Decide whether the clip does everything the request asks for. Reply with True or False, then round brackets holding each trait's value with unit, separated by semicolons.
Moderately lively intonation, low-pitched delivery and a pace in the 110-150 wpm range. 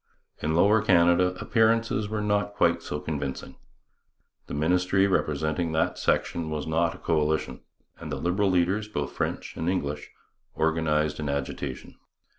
True (4.1 semitones; 85 Hz; 140 wpm)